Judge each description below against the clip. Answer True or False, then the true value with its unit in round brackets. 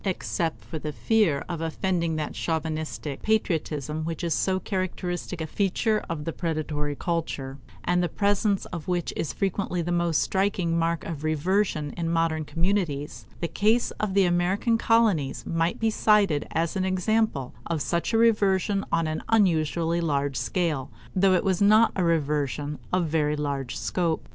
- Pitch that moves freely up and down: False (3.6 semitones)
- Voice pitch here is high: False (170 Hz)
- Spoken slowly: False (165 wpm)